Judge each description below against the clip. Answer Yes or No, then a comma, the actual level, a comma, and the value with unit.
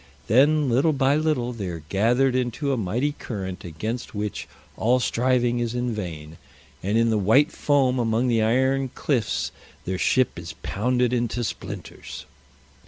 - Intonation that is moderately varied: Yes, average, 3.6 semitones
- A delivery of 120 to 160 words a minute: Yes, average, 155 wpm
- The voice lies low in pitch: Yes, low, 120 Hz